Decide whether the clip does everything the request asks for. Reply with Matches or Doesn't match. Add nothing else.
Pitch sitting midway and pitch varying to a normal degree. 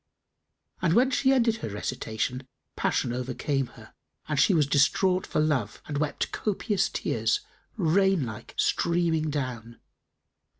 Doesn't match